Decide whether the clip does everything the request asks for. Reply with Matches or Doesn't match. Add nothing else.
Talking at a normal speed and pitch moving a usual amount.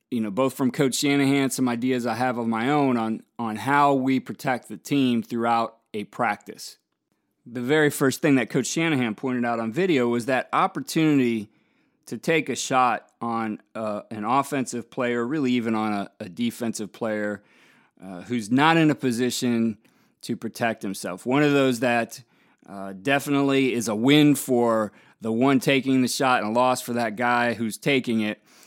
Matches